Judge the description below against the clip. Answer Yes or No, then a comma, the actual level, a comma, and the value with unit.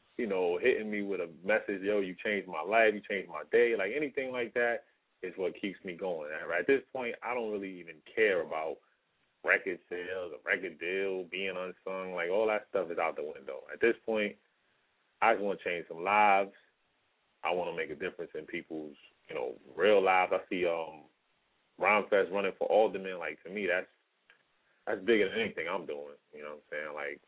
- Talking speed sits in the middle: No, fast, 215 wpm